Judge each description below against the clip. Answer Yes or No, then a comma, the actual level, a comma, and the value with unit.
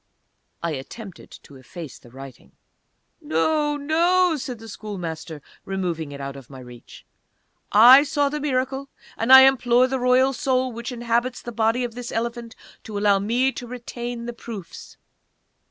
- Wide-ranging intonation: Yes, wide, 6.2 semitones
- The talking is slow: No, average, 155 wpm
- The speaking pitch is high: Yes, high, 235 Hz